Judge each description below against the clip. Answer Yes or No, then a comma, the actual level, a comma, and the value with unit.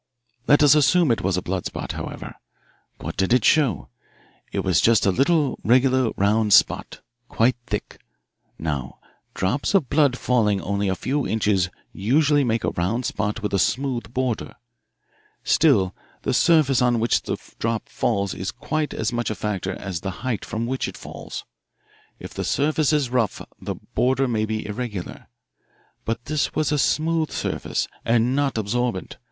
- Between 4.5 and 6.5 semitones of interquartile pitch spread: Yes, average, 5.1 semitones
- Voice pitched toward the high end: No, low, 120 Hz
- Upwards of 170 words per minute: No, average, 165 wpm